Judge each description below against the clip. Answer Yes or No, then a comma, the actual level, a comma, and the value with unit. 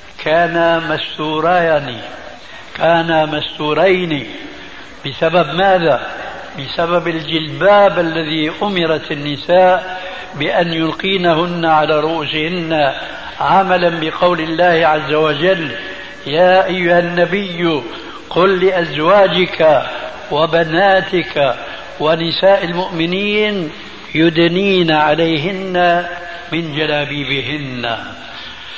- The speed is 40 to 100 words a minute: Yes, slow, 65 wpm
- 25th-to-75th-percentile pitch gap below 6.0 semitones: Yes, average, 2.8 semitones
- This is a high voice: No, medium, 170 Hz